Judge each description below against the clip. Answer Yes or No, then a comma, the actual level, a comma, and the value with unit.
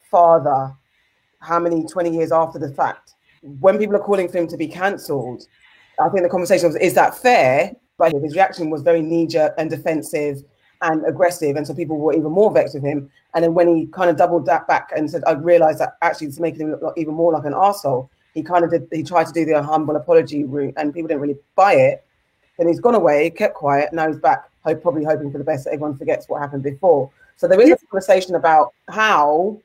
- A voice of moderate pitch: Yes, medium, 165 Hz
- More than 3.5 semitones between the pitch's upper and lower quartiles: No, average, 2.7 semitones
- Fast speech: Yes, fast, 230 wpm